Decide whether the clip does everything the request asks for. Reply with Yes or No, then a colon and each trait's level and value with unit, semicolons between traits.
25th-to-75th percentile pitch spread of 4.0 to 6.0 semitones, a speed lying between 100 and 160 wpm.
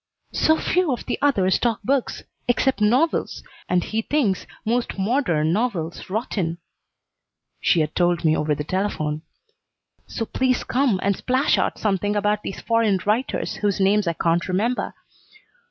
Yes: wide, 5.6 semitones; average, 150 wpm